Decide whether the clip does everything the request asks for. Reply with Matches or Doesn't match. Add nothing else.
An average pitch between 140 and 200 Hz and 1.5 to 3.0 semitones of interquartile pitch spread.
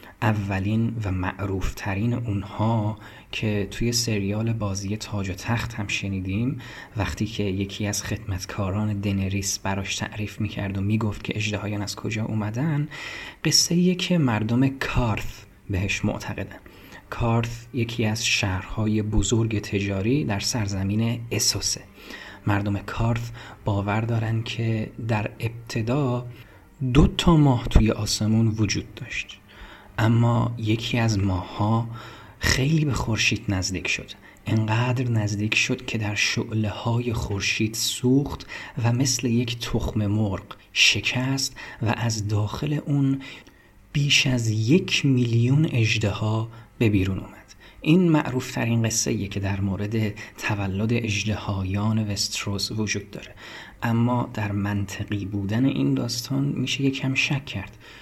Doesn't match